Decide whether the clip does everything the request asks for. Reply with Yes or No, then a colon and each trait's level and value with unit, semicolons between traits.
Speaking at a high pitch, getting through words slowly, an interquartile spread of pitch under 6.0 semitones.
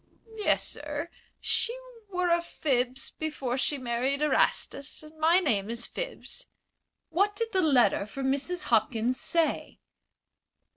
Yes: very high, 295 Hz; slow, 130 wpm; wide, 5.5 semitones